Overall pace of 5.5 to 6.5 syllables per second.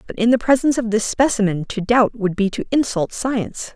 Yes: 5.7 syllables/s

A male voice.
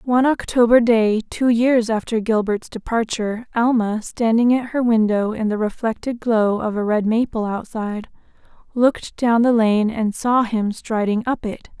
No: female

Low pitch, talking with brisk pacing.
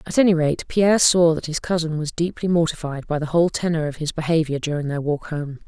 No: medium, 160 Hz; fast, 235 wpm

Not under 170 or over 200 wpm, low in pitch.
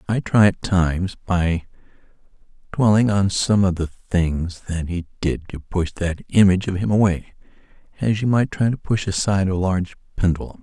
Yes: average, 175 wpm; very low, 95 Hz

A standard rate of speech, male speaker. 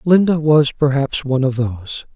Yes: average, 165 wpm; male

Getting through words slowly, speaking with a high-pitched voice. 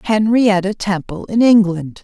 Yes: slow, 120 wpm; high, 200 Hz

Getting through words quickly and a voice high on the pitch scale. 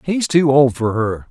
No: fast, 230 wpm; low, 135 Hz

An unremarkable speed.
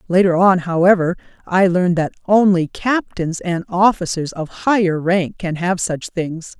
Yes: average, 155 wpm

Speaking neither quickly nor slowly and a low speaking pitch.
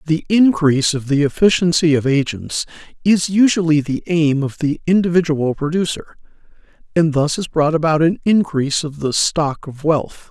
No: average, 155 wpm; medium, 155 Hz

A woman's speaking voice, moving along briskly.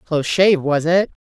Yes: female; fast, 245 wpm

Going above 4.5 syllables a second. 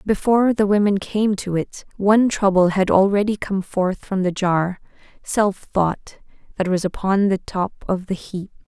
No: 4.4 syllables/s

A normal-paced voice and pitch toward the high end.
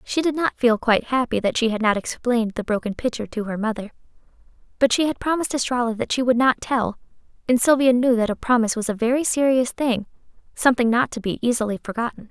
No: fast, 215 wpm; high, 240 Hz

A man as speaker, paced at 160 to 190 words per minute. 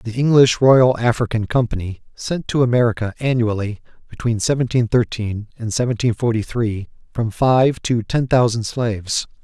No: male; average, 140 wpm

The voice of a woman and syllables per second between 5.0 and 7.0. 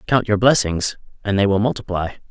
No: male; 5.5 syllables/s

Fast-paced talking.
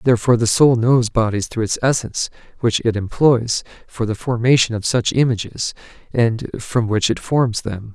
No: average, 175 wpm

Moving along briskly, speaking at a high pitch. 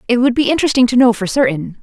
Yes: fast, 265 wpm; high, 240 Hz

